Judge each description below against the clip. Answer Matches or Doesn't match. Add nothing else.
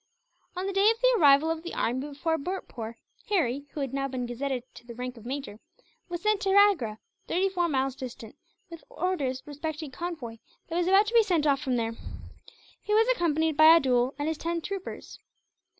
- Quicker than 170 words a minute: Matches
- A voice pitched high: Matches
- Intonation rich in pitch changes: Matches